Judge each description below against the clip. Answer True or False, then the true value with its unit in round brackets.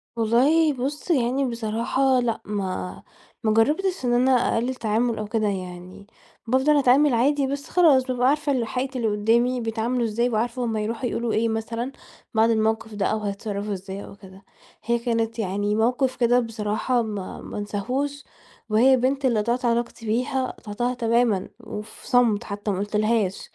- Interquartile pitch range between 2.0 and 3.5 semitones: True (3.0 semitones)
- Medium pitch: False (230 Hz)